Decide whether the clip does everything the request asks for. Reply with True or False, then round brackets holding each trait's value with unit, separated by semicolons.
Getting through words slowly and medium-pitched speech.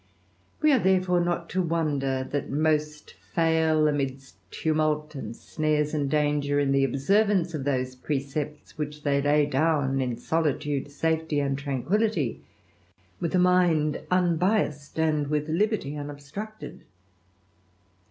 True (125 wpm; 150 Hz)